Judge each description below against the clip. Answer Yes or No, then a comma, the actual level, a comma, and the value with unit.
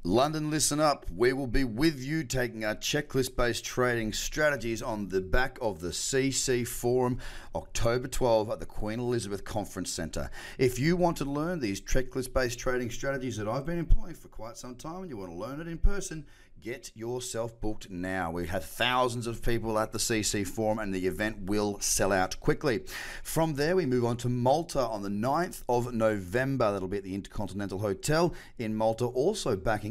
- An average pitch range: Yes, average, 4.4 semitones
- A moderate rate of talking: Yes, average, 195 wpm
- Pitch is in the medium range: No, low, 120 Hz